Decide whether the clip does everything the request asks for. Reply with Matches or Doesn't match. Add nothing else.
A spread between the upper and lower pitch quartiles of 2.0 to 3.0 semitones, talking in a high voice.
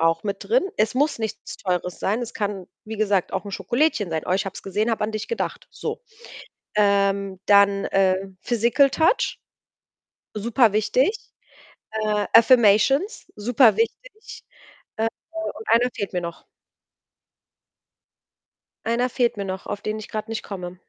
Doesn't match